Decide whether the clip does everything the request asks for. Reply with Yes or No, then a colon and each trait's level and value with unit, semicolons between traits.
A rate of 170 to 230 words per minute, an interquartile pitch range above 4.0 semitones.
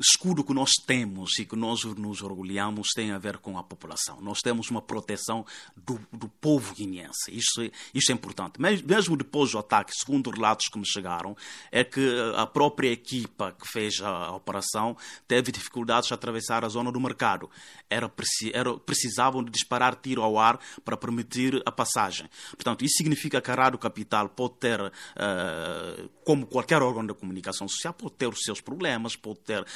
No: average, 175 wpm; average, 3.5 semitones